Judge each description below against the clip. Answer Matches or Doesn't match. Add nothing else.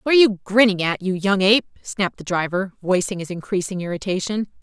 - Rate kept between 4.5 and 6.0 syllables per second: Doesn't match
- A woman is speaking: Matches